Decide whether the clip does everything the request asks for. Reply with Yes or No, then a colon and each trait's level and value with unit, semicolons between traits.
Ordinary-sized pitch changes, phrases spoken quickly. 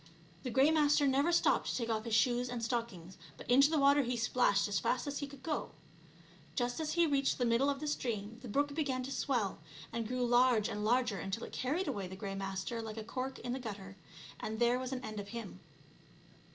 Yes: average, 4.0 semitones; fast, 230 wpm